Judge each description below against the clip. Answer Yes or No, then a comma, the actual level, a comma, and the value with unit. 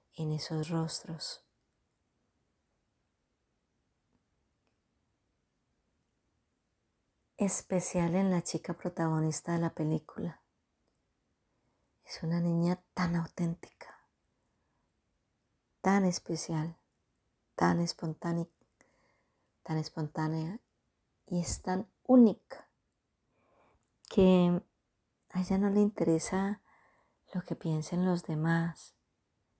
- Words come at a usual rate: No, slow, 75 wpm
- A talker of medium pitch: Yes, medium, 170 Hz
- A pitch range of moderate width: No, narrow, 2.3 semitones